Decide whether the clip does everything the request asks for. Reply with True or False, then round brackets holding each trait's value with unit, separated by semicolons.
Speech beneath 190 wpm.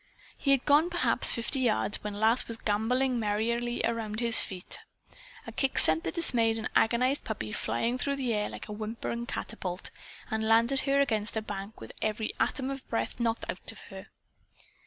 True (180 wpm)